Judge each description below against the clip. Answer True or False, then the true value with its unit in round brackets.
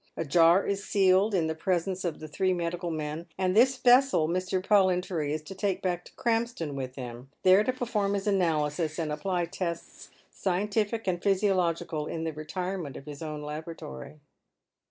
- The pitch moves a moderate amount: True (3.9 semitones)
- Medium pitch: True (175 Hz)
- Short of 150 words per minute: False (175 wpm)